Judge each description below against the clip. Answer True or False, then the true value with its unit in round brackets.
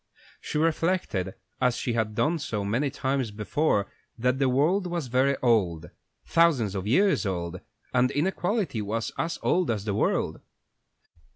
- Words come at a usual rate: True (150 wpm)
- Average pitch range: False (7.3 semitones)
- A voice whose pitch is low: True (125 Hz)